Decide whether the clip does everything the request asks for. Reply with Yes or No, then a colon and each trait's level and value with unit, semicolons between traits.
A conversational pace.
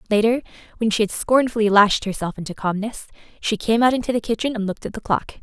No: fast, 220 wpm